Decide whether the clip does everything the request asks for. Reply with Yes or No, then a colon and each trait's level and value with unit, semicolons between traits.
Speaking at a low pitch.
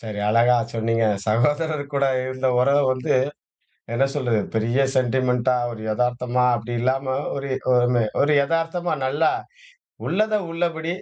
Yes: low, 130 Hz